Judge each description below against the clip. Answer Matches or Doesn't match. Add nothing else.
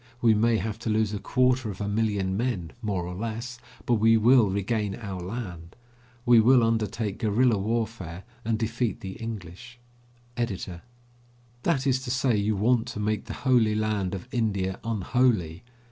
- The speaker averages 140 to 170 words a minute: Matches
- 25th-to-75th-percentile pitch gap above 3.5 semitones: Doesn't match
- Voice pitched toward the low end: Matches